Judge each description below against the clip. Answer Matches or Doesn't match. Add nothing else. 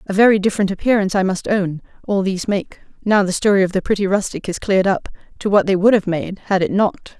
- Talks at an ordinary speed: Doesn't match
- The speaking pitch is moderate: Doesn't match